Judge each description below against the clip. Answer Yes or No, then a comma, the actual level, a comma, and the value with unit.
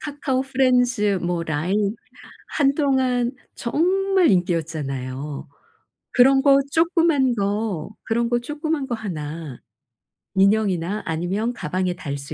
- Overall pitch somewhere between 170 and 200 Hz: No, high, 220 Hz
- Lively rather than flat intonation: Yes, wide, 7.6 semitones